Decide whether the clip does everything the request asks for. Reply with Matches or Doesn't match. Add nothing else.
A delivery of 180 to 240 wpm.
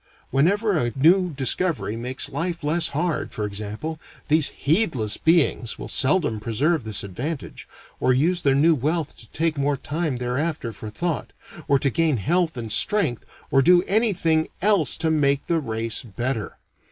Doesn't match